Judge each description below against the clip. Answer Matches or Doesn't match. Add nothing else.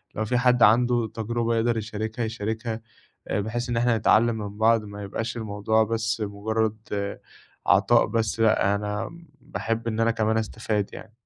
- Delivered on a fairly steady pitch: Matches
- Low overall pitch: Matches